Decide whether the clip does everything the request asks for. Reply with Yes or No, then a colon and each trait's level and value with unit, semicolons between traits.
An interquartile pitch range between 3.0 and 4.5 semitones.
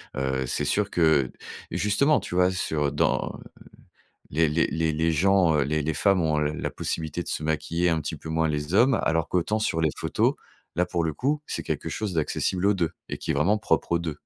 Yes: average, 3.4 semitones